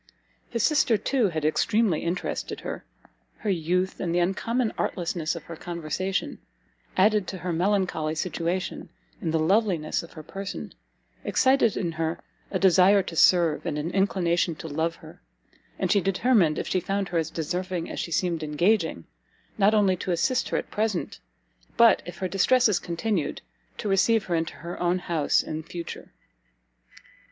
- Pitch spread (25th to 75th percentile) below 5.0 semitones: Yes, average, 3.3 semitones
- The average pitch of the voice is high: No, medium, 180 Hz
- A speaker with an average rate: Yes, average, 165 wpm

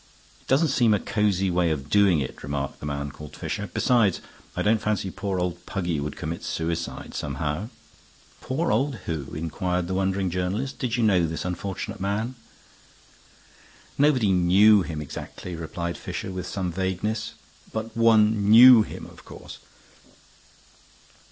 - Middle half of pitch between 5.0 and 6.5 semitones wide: No, average, 4.3 semitones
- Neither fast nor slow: Yes, average, 150 wpm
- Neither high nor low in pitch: No, very low, 95 Hz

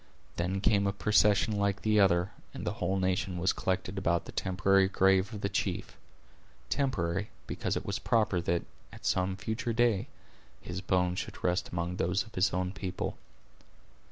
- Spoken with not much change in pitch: Yes, narrow, 1.9 semitones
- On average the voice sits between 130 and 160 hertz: No, very low, 95 Hz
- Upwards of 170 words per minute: No, average, 165 wpm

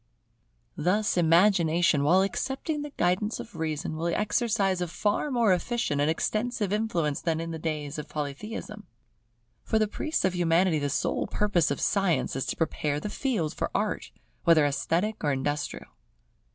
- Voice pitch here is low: No, medium, 175 Hz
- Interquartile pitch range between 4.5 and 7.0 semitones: Yes, average, 5.2 semitones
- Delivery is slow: No, average, 160 wpm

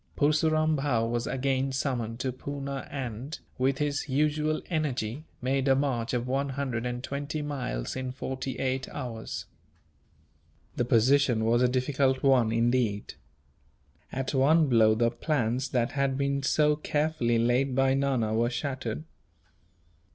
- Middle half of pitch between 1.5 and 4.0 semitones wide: Yes, average, 2.9 semitones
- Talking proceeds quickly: No, average, 140 wpm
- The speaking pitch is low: Yes, low, 130 Hz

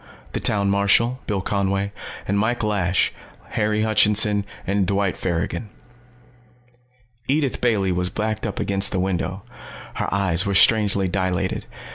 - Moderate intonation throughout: No, narrow, 2.0 semitones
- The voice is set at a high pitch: No, low, 100 Hz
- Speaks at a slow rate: Yes, slow, 130 wpm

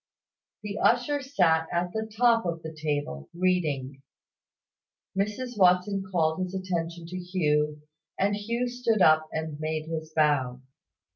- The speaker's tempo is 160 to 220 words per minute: No, slow, 135 wpm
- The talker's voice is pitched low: No, medium, 175 Hz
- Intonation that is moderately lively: Yes, average, 4.6 semitones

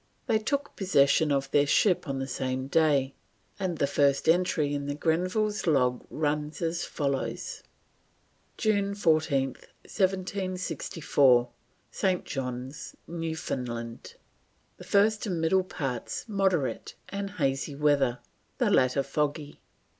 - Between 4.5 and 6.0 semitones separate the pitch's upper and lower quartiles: Yes, average, 5.2 semitones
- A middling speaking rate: No, slow, 115 wpm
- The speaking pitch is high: No, medium, 150 Hz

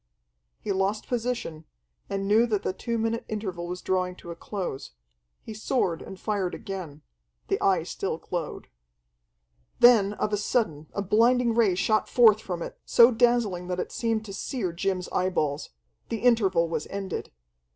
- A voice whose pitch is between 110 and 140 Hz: No, high, 195 Hz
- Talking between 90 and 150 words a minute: No, average, 160 wpm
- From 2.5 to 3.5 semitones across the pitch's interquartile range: No, average, 3.9 semitones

